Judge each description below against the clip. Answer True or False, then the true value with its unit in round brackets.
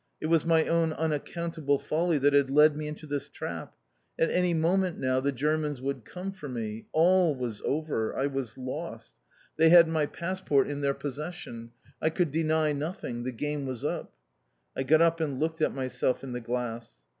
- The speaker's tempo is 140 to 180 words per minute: False (190 wpm)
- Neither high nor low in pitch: True (150 Hz)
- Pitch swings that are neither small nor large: True (3.7 semitones)